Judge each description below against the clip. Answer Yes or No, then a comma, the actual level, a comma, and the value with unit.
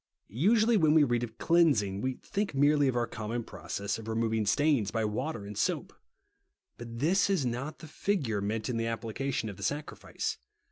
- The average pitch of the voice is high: No, low, 120 Hz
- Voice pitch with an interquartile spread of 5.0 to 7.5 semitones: Yes, wide, 5.4 semitones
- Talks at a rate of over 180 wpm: Yes, average, 195 wpm